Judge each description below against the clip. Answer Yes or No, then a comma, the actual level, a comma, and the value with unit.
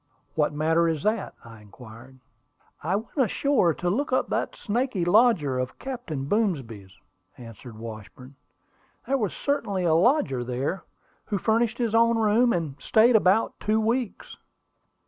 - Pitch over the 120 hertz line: Yes, medium, 185 Hz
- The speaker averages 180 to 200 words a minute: No, average, 145 wpm